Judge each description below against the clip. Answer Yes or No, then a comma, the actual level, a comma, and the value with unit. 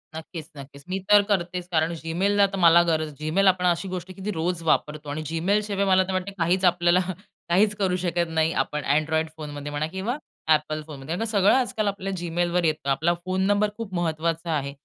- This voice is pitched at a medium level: Yes, medium, 175 Hz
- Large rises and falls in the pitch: No, average, 3.2 semitones